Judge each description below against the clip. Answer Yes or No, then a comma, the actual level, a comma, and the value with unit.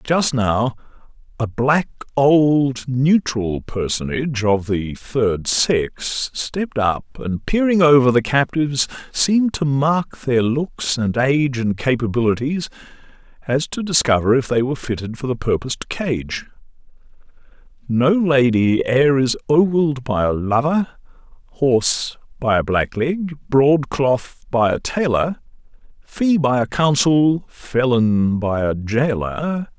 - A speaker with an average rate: No, slow, 125 wpm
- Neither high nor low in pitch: No, low, 130 Hz